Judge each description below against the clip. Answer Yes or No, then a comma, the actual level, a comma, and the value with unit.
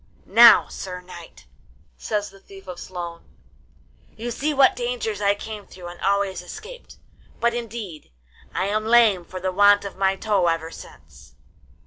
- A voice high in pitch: Yes, high, 200 Hz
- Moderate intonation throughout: Yes, average, 3.6 semitones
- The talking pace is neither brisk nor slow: Yes, average, 155 wpm